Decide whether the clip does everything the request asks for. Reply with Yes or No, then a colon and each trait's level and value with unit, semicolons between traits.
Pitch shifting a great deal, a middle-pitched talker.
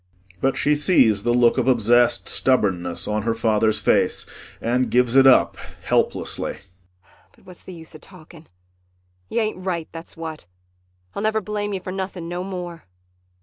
Yes: wide, 7.3 semitones; medium, 155 Hz